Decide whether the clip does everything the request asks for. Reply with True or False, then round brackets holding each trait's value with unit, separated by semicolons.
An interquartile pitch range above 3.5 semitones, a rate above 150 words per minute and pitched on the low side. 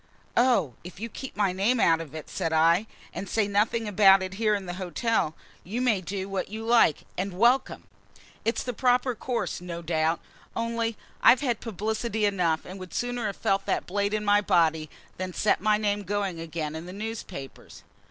False (4.1 semitones; 190 wpm; 200 Hz)